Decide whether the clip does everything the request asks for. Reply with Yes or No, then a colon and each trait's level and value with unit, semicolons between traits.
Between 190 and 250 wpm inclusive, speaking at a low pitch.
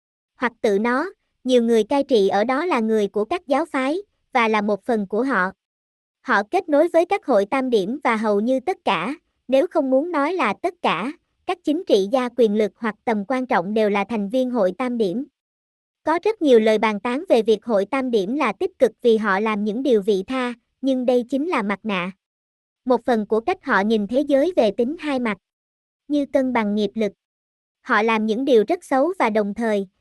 No: average, 220 wpm; high, 245 Hz